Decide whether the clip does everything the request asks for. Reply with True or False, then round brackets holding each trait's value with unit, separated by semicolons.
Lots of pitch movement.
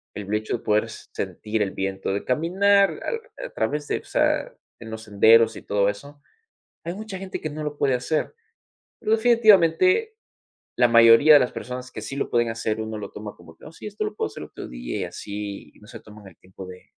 True (7.9 semitones)